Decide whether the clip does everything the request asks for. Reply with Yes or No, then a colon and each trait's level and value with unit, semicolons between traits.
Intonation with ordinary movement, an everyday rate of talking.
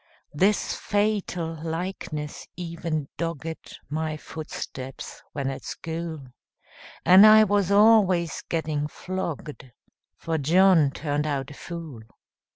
No: average, 3.8 semitones; slow, 105 wpm